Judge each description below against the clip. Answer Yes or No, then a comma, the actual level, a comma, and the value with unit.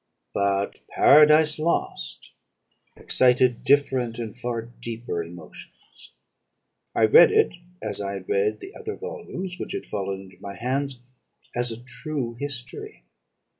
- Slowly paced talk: Yes, slow, 130 wpm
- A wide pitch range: Yes, wide, 6.2 semitones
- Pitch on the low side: Yes, low, 120 Hz